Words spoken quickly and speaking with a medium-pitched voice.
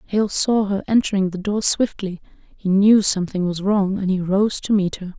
No: fast, 210 wpm; high, 195 Hz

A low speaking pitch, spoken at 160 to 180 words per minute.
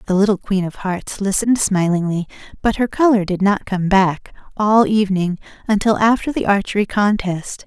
No: high, 200 Hz; average, 165 wpm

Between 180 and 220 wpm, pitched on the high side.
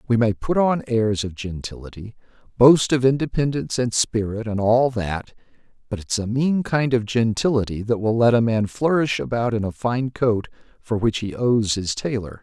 No: average, 190 wpm; low, 115 Hz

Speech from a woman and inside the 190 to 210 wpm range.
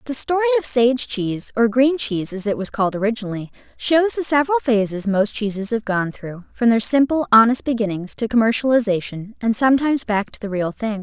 Yes: female; average, 195 wpm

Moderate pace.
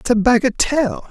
Yes: average, 165 wpm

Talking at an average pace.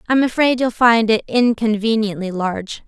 Yes: average, 145 wpm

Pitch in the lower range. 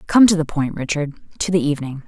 No: medium, 160 Hz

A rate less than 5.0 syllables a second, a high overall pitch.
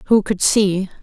Yes: 4.2 syllables/s; high, 200 Hz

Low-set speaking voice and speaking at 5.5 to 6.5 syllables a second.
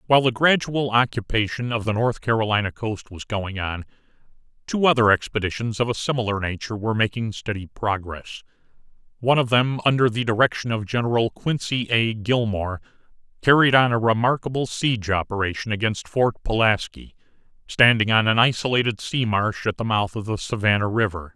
Yes: low, 110 Hz; 5.6 syllables/s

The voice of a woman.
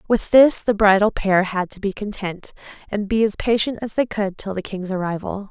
Yes: female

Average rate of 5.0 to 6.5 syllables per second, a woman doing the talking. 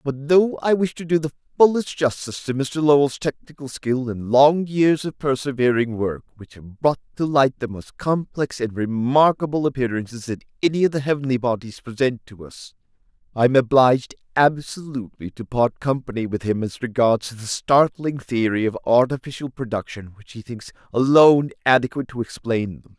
No: 5.2 syllables/s; male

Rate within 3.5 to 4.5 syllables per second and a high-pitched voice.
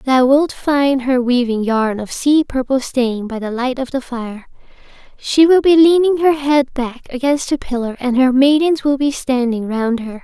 Yes: 4.4 syllables/s; very high, 260 Hz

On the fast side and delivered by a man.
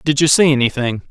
Yes: fast, 220 wpm; male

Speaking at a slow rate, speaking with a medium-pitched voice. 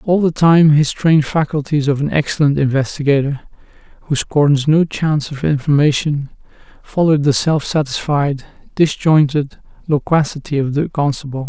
Yes: slow, 130 wpm; medium, 145 Hz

